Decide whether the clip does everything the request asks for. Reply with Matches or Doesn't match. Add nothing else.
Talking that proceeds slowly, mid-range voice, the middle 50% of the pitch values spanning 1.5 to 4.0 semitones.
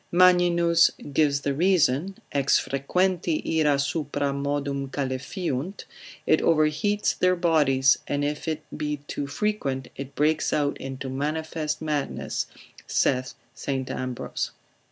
Matches